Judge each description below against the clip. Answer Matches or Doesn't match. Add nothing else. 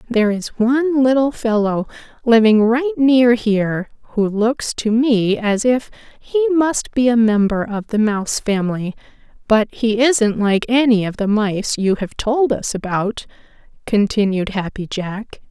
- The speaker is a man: Doesn't match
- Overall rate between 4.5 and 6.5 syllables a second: Doesn't match